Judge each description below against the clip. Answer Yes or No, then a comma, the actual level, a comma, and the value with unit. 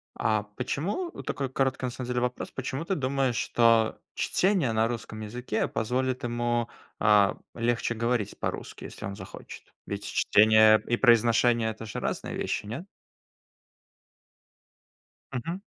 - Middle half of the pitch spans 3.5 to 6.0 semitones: No, average, 2.7 semitones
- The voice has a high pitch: No, low, 120 Hz